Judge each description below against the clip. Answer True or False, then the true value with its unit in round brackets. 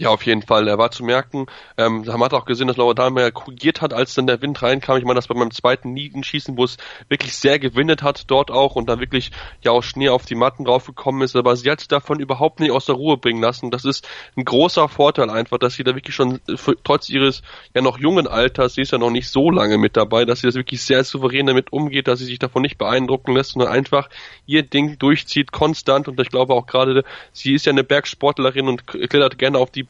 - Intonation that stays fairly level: True (2.1 semitones)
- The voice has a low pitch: True (130 Hz)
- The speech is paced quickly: True (250 wpm)